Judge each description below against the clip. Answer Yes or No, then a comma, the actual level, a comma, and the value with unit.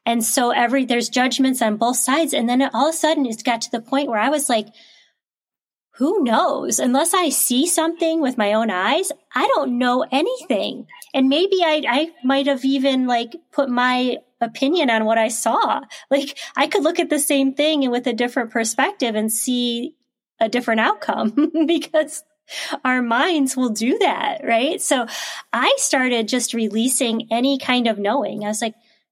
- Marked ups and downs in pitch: No, average, 4.0 semitones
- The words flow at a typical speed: Yes, average, 185 wpm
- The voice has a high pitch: Yes, very high, 255 Hz